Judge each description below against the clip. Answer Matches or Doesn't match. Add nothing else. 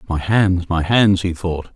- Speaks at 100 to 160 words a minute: Doesn't match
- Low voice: Matches